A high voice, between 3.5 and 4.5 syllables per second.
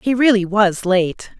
Yes: high, 205 Hz; 4.0 syllables/s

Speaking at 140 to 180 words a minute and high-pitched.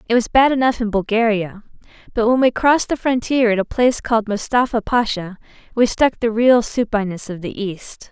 No: average, 190 wpm; high, 225 Hz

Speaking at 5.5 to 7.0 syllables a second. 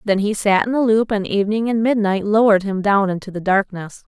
Yes: 5.8 syllables/s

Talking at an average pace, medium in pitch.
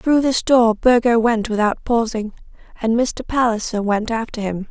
No: average, 165 wpm; high, 230 Hz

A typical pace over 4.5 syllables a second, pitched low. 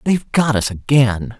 Yes: 4.7 syllables/s; low, 120 Hz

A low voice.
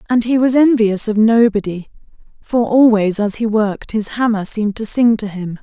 No: high, 220 Hz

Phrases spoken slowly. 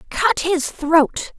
Yes: slow, 130 wpm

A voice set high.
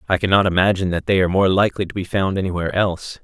No: very low, 95 Hz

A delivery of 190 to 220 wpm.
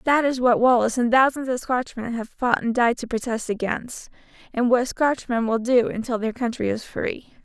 Yes: average, 200 wpm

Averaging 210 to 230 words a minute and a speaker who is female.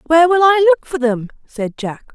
Yes: fast, 225 wpm; female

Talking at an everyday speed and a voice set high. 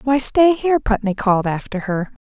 Yes: average, 185 wpm; high, 230 Hz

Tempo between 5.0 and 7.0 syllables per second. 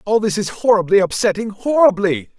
Yes: 5.5 syllables/s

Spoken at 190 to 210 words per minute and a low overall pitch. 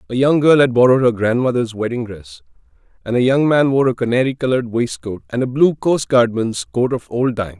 Yes: fast, 205 wpm; low, 125 Hz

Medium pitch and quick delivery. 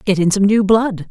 No: high, 200 Hz; fast, 270 wpm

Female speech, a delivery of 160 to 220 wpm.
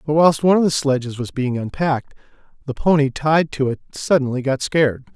No: male; average, 200 wpm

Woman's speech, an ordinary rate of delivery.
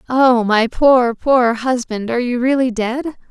Yes: female; average, 165 wpm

